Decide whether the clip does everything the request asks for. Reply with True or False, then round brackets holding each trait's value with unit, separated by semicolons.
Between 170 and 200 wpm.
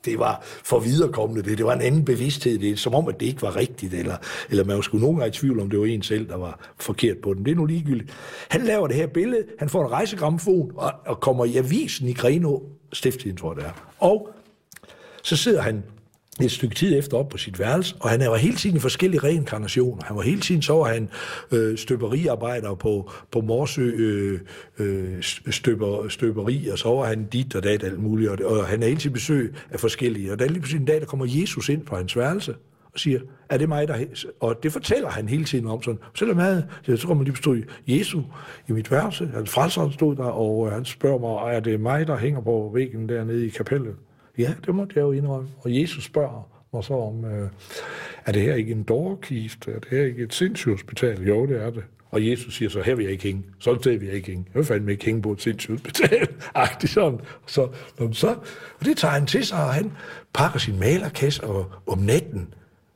False (225 wpm)